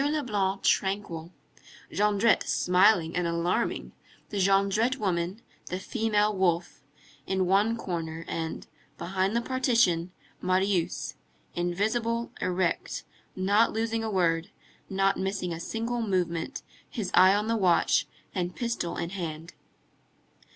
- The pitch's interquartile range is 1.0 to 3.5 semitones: No, average, 4.0 semitones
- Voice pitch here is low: No, high, 190 Hz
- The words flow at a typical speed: No, slow, 115 wpm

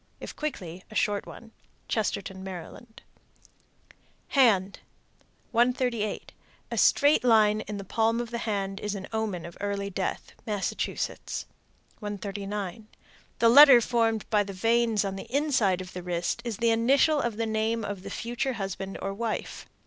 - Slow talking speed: No, average, 150 wpm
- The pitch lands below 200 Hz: No, high, 215 Hz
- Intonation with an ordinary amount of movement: Yes, average, 3.1 semitones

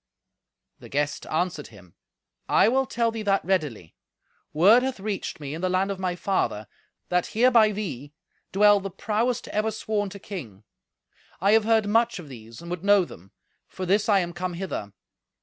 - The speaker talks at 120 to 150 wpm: No, average, 180 wpm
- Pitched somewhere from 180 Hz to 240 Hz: Yes, high, 190 Hz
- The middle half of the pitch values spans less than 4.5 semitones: No, average, 4.9 semitones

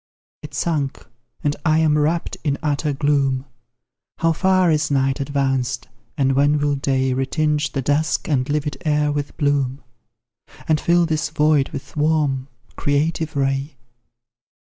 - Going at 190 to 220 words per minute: No, average, 140 wpm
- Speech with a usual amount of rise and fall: No, narrow, 2.1 semitones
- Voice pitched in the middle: Yes, medium, 145 Hz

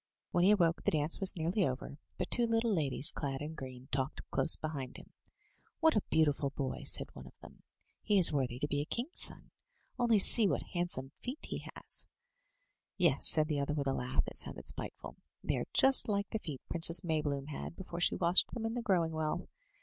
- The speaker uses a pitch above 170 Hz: No, medium, 160 Hz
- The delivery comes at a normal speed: No, fast, 210 wpm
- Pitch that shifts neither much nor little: No, wide, 5.8 semitones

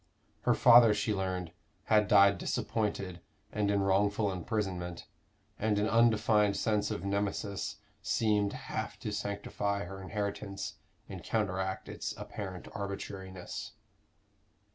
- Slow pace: Yes, slow, 115 wpm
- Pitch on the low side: Yes, low, 100 Hz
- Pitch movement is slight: Yes, narrow, 1.6 semitones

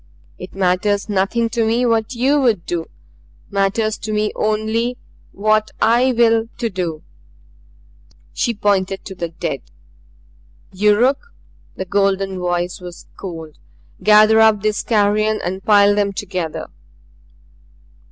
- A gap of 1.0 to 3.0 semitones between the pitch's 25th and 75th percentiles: Yes, average, 2.7 semitones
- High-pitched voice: Yes, high, 205 Hz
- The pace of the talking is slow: Yes, slow, 125 wpm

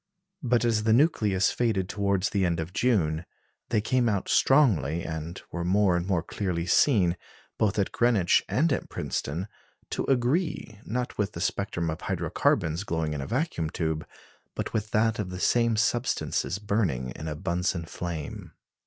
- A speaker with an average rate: Yes, average, 170 wpm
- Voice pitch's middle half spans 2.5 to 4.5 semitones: No, average, 5.2 semitones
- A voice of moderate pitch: No, low, 100 Hz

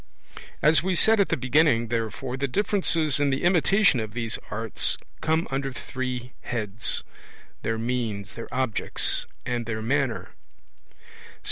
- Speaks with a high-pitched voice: No, low, 125 Hz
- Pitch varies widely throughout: No, average, 4.8 semitones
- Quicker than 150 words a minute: No, slow, 135 wpm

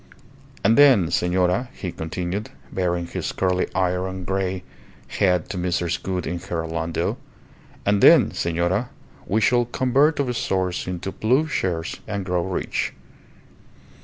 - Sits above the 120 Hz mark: No, very low, 95 Hz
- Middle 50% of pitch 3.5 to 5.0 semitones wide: No, average, 2.9 semitones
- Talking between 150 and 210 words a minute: No, slow, 135 wpm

